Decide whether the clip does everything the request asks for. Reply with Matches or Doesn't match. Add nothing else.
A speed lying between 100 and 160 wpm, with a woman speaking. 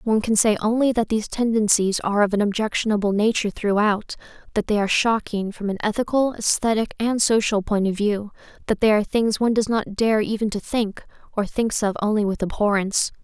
Doesn't match